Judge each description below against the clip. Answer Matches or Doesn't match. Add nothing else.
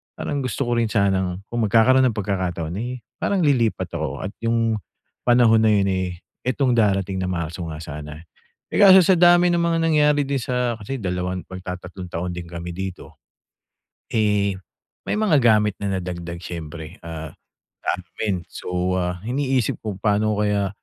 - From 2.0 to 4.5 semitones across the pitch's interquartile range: Doesn't match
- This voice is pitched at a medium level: Doesn't match